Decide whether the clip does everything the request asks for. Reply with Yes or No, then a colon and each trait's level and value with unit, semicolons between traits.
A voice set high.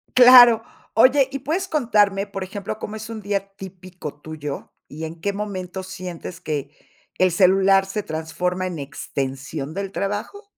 Yes: high, 195 Hz